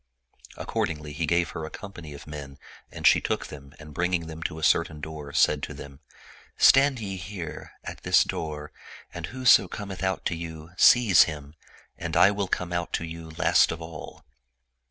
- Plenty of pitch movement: No, average, 3.3 semitones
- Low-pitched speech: Yes, very low, 80 Hz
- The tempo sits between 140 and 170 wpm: No, average, 190 wpm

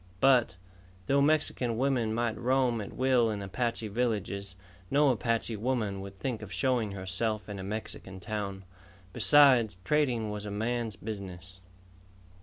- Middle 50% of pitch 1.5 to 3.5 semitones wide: No, average, 3.9 semitones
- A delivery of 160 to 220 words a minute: No, average, 140 wpm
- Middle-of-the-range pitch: No, low, 110 Hz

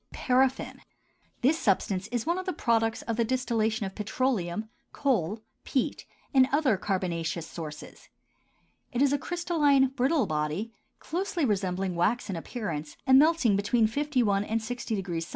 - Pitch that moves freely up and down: Yes, wide, 5.7 semitones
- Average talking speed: Yes, average, 145 wpm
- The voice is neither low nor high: No, high, 225 Hz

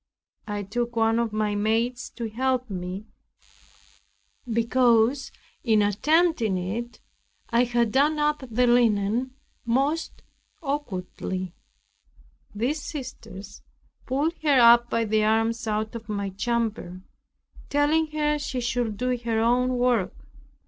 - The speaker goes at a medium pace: No, slow, 115 wpm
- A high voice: Yes, high, 235 Hz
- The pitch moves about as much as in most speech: Yes, average, 3.2 semitones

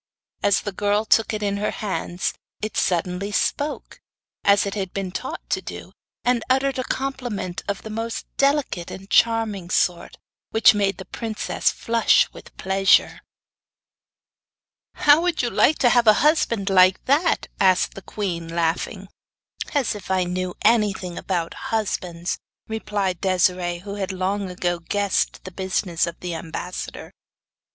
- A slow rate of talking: No, average, 150 wpm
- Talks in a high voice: Yes, high, 200 Hz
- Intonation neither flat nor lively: Yes, average, 3.5 semitones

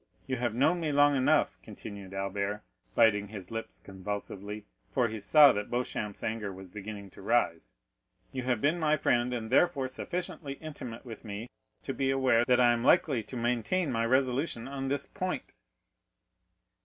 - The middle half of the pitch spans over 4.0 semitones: Yes, average, 4.5 semitones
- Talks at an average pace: Yes, average, 165 wpm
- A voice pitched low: Yes, low, 120 Hz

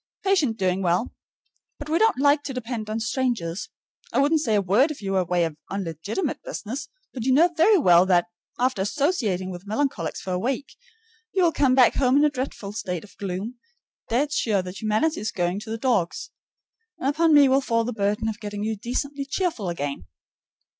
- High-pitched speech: Yes, high, 225 Hz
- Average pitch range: No, wide, 6.5 semitones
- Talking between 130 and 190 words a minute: No, average, 200 wpm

